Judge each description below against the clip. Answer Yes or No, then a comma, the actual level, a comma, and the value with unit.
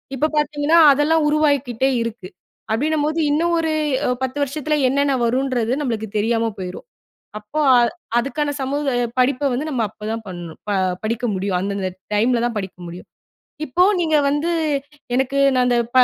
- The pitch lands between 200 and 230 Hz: No, very high, 255 Hz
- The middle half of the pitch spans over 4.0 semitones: Yes, average, 4.7 semitones